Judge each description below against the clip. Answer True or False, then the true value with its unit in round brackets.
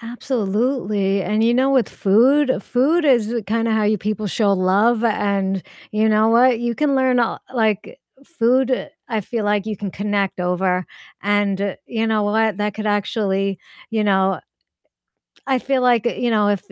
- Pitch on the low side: False (215 Hz)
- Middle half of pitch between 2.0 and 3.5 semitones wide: True (3.0 semitones)